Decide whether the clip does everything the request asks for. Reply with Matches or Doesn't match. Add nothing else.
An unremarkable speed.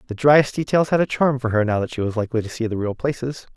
Doesn't match